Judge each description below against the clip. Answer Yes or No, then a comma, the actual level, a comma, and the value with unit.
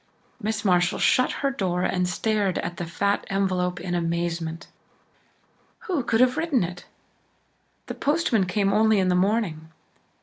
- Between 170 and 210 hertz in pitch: Yes, high, 190 Hz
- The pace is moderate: Yes, average, 145 wpm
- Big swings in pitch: No, average, 3.9 semitones